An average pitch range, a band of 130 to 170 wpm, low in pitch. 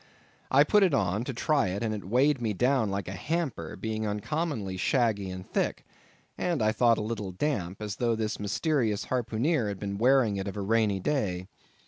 No: average, 4.8 semitones; average, 195 wpm; low, 110 Hz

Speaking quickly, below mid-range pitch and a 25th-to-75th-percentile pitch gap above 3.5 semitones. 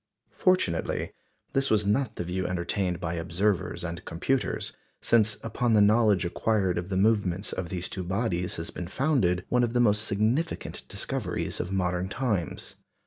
No: average, 160 wpm; low, 100 Hz; average, 4.1 semitones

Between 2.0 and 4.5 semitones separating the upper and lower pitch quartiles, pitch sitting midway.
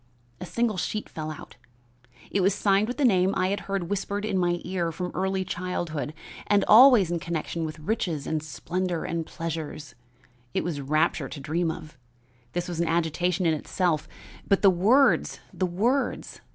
Yes: average, 3.4 semitones; medium, 175 Hz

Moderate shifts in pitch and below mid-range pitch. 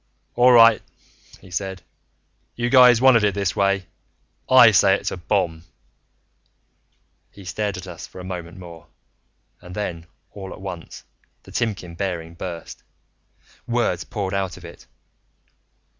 Yes: average, 3.1 semitones; very low, 95 Hz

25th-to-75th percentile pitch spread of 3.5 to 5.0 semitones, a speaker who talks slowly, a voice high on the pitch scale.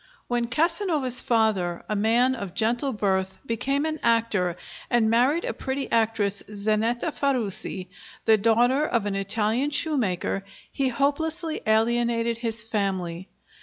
Yes: average, 4.2 semitones; slow, 130 wpm; high, 230 Hz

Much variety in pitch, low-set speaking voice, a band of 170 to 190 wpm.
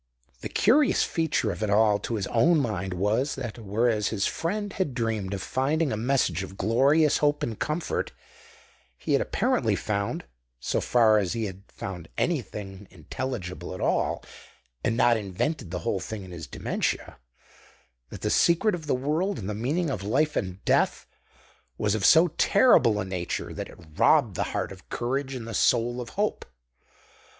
Yes: wide, 6.8 semitones; low, 115 Hz; average, 175 wpm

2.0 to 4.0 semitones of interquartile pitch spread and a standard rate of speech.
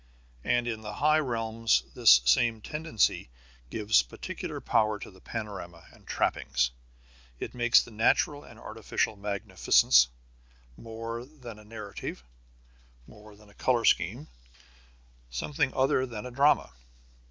No: average, 2.8 semitones; slow, 130 wpm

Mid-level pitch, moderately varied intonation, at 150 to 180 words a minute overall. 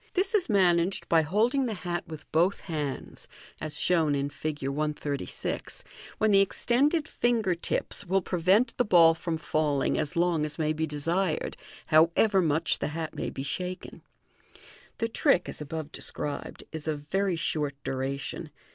Yes: medium, 165 Hz; average, 4.3 semitones; average, 155 wpm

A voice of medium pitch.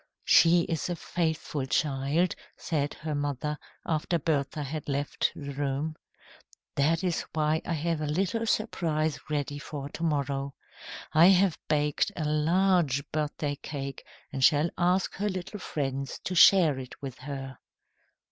Yes: medium, 150 Hz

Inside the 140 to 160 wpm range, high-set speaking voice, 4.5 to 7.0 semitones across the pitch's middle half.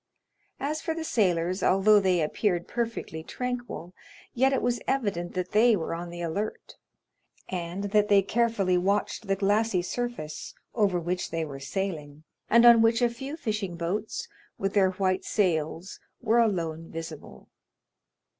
Yes: average, 150 wpm; high, 195 Hz; average, 4.8 semitones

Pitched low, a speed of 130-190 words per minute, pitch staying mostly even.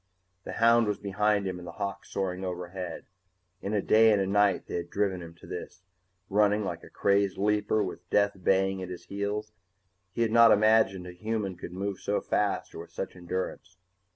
No: low, 100 Hz; average, 200 wpm; narrow, 2.2 semitones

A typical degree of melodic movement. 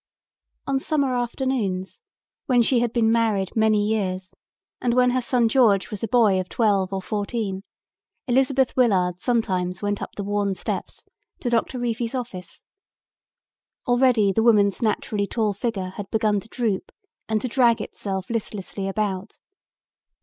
Yes: average, 3.6 semitones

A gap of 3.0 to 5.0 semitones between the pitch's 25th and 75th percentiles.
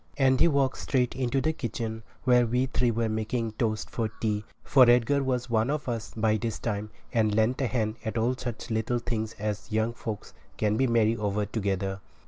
No: narrow, 2.4 semitones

